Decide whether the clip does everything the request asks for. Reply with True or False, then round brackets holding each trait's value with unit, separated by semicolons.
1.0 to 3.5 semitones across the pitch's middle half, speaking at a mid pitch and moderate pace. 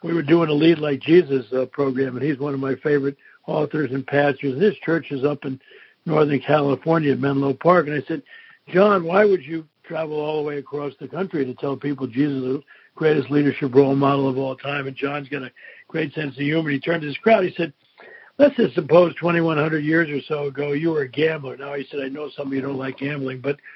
False (2.8 semitones; 145 Hz; 245 wpm)